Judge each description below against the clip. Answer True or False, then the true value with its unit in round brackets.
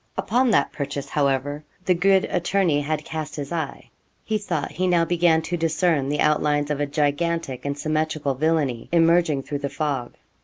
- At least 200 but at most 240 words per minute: False (175 wpm)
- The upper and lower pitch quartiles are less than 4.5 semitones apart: True (2.9 semitones)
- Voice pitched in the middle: True (155 Hz)